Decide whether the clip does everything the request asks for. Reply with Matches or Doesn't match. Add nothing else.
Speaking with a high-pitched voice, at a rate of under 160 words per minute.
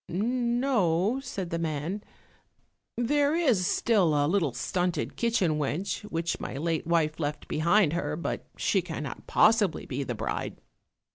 Doesn't match